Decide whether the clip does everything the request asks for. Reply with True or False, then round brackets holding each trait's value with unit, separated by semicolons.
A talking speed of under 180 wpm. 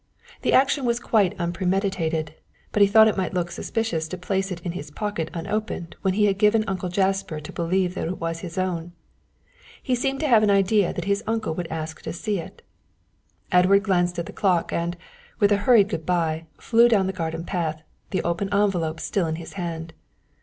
False (200 wpm)